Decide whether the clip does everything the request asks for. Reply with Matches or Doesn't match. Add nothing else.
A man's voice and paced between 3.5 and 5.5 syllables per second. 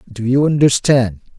Matches